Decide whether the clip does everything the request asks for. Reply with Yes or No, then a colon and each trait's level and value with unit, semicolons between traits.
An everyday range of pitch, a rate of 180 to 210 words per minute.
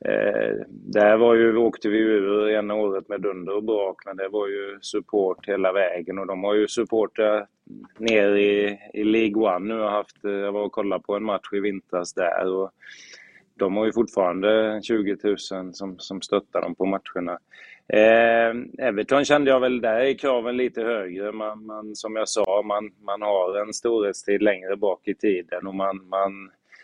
No: narrow, 2.0 semitones; average, 185 wpm